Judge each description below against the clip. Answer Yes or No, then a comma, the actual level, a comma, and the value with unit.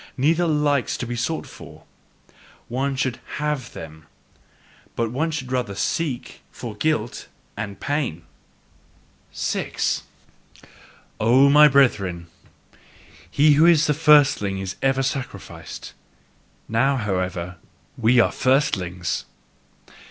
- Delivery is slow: Yes, slow, 105 wpm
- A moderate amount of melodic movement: No, wide, 5.9 semitones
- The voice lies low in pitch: Yes, low, 130 Hz